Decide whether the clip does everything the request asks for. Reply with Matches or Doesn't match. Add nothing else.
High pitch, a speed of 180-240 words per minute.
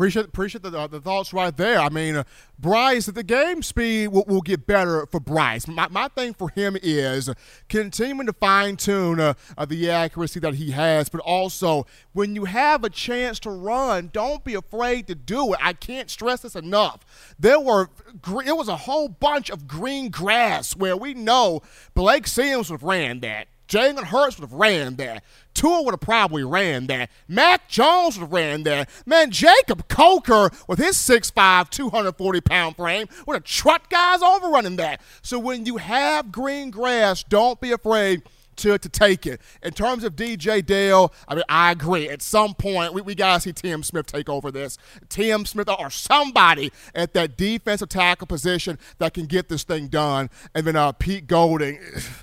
Matches